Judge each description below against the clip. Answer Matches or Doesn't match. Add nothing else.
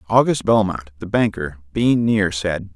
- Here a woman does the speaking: Doesn't match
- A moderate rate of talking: Matches